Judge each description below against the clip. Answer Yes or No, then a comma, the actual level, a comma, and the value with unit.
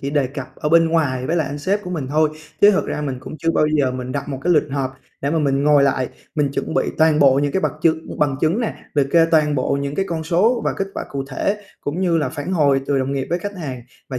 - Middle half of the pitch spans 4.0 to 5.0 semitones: No, average, 3.2 semitones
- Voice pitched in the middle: Yes, medium, 150 Hz